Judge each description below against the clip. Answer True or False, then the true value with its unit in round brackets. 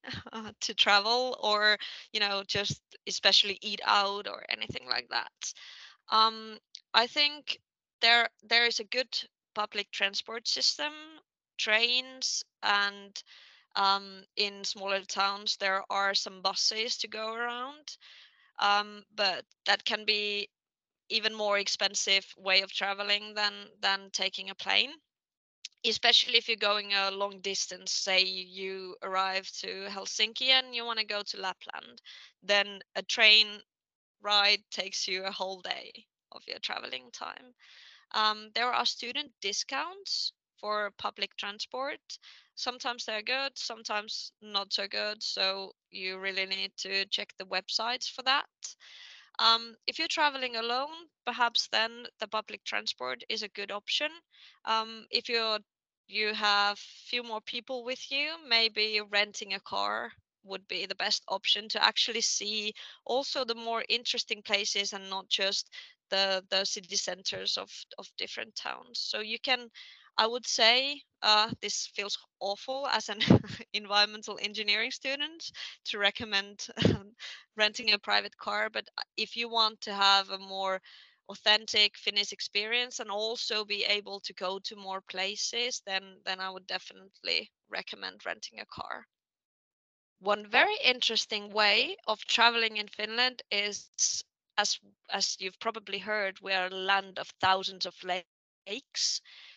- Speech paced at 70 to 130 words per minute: False (140 wpm)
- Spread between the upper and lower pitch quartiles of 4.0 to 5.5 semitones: False (2.8 semitones)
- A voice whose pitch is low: False (210 Hz)